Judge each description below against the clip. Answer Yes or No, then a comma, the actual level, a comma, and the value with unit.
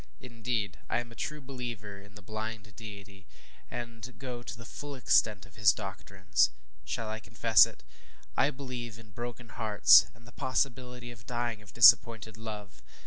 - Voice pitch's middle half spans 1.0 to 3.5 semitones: Yes, average, 2.7 semitones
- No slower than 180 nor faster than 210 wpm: No, average, 165 wpm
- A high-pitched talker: No, low, 115 Hz